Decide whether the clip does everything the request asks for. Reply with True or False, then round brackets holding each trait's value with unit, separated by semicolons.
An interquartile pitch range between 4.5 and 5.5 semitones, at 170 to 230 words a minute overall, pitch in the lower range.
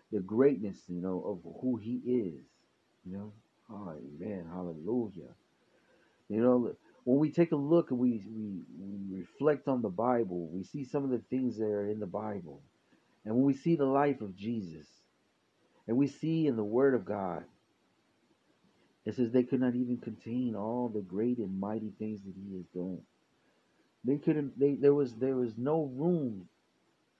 True (4.9 semitones; 180 wpm; 120 Hz)